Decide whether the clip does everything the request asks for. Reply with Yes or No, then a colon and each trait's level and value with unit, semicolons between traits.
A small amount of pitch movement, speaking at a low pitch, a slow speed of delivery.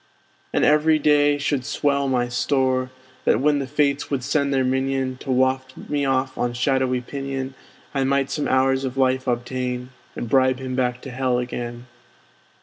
No: narrow, 1.4 semitones; low, 130 Hz; average, 170 wpm